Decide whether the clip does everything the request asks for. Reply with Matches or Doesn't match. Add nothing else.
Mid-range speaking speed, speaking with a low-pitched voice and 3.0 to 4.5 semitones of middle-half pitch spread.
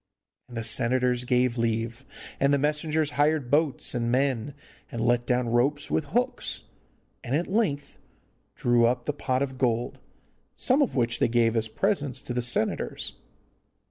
Matches